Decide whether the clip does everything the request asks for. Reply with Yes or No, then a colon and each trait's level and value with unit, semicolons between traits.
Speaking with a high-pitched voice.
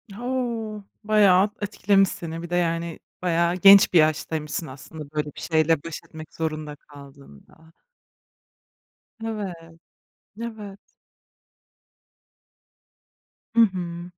No: medium, 170 Hz